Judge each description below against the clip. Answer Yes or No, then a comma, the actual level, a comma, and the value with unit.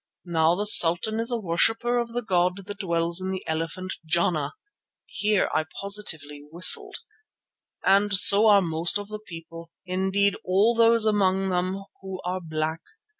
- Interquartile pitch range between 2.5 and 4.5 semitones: Yes, average, 3.6 semitones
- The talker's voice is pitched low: No, medium, 185 Hz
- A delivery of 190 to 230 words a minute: No, average, 155 wpm